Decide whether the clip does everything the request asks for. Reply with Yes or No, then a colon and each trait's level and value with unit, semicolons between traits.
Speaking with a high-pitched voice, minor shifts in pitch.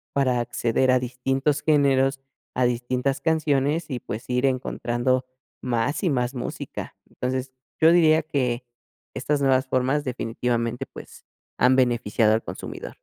No: low, 130 Hz; narrow, 2.2 semitones